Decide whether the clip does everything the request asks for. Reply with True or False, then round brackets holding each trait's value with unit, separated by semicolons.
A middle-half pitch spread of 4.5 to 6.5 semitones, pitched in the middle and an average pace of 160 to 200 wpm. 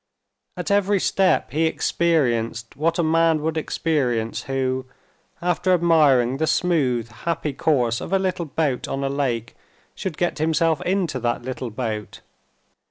False (5.0 semitones; 150 Hz; 145 wpm)